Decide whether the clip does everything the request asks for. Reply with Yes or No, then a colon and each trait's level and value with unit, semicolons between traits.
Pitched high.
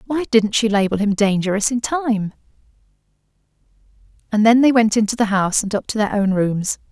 Yes: high, 215 Hz